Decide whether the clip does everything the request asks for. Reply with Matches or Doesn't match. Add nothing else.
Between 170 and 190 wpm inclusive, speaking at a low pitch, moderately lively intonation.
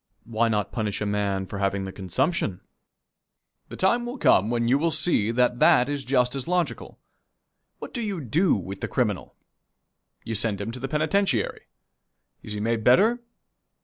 Doesn't match